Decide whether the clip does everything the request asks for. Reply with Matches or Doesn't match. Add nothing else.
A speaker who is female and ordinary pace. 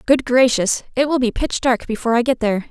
Doesn't match